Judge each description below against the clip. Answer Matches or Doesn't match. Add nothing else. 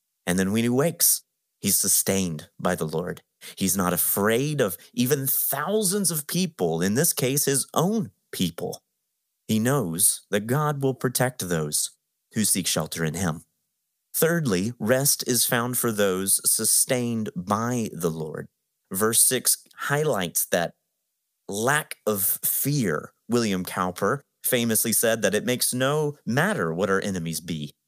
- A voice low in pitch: Matches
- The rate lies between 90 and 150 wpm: Matches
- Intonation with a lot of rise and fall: Matches